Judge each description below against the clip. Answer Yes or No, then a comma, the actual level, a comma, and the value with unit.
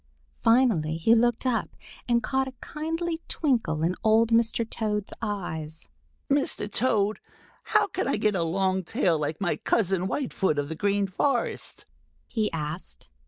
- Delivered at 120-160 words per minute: Yes, average, 150 wpm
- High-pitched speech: Yes, high, 210 Hz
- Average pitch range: No, wide, 5.7 semitones